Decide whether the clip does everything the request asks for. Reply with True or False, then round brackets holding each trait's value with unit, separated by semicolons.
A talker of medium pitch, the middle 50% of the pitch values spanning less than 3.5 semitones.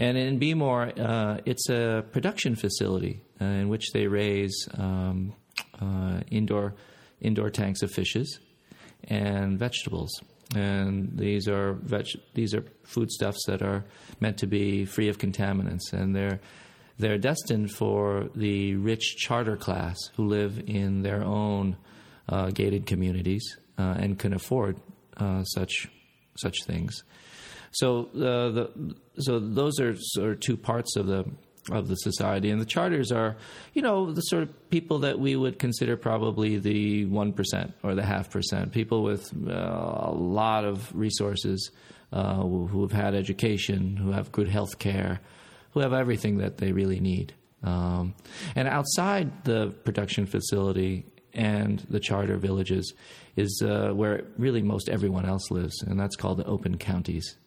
False (105 Hz; 2.5 semitones)